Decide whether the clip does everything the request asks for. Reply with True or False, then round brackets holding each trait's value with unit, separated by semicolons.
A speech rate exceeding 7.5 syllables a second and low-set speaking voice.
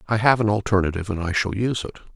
True (7.9 syllables/s; 105 Hz)